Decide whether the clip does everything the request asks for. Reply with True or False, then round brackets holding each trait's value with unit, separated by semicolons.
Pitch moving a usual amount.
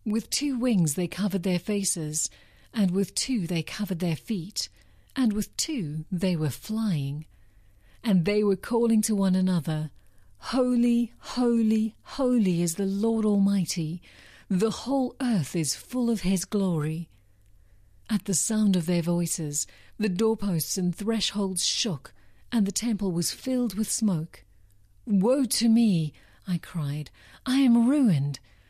False (6.0 semitones)